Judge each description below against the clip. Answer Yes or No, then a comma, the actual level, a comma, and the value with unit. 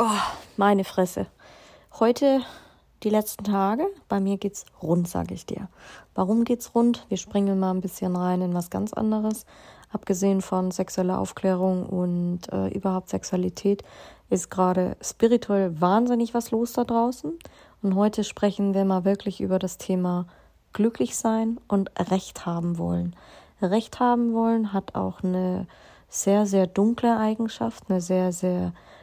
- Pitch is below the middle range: No, high, 195 Hz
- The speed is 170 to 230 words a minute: No, average, 145 wpm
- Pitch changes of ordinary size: Yes, average, 3.3 semitones